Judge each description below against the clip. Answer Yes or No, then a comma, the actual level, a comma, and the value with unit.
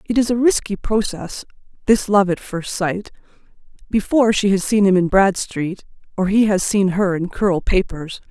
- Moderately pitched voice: No, high, 200 Hz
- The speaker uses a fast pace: No, average, 180 wpm